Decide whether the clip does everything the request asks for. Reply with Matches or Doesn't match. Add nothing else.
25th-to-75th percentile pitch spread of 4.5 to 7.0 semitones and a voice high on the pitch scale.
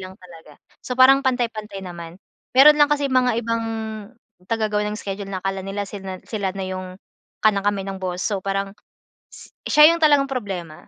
Matches